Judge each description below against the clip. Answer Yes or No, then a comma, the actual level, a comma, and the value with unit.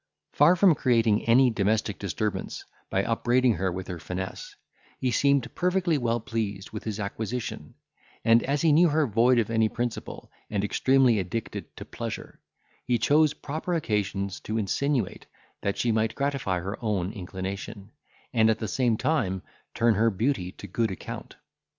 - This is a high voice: No, low, 115 Hz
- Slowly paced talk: No, average, 160 wpm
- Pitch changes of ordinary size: Yes, average, 4.5 semitones